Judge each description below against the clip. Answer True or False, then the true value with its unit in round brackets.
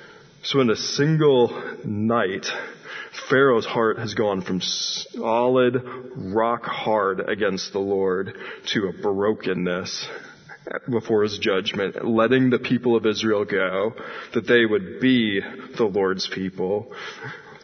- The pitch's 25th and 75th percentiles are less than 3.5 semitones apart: False (3.8 semitones)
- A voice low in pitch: True (115 Hz)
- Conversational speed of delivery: False (120 wpm)